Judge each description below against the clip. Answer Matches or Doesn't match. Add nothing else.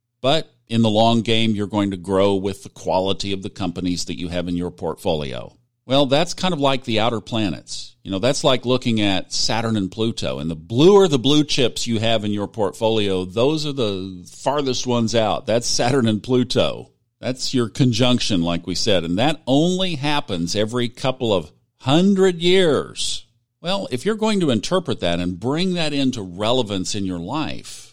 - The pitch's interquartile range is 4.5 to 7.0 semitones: Matches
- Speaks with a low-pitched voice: Matches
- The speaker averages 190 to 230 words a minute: Matches